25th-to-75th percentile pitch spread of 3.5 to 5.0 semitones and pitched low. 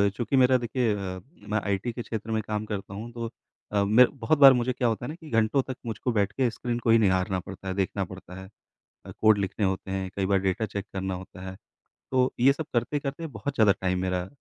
Yes: average, 4.1 semitones; low, 110 Hz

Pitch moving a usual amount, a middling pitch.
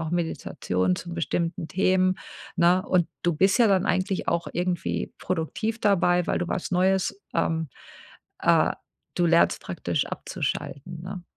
No: narrow, 1.9 semitones; medium, 175 Hz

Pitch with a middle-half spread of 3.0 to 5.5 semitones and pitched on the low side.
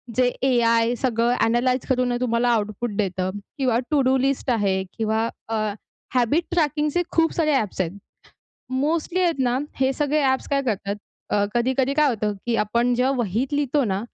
No: average, 3.5 semitones; very high, 250 Hz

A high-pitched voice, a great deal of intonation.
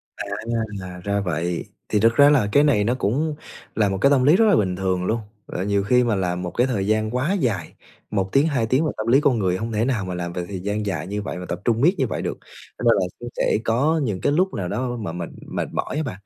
No: low, 110 Hz; wide, 6.0 semitones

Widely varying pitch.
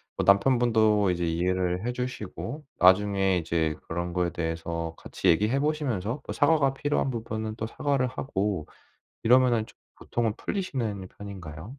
Yes: wide, 6.0 semitones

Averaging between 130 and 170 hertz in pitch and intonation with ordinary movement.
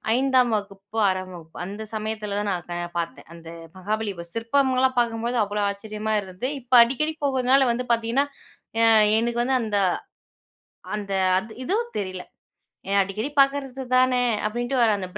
No: high, 225 Hz; average, 4.2 semitones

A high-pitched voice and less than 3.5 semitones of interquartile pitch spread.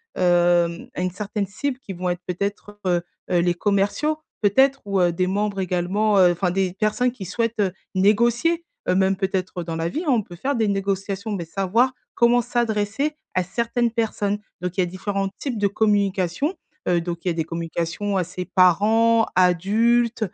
No: high, 195 Hz; average, 3.9 semitones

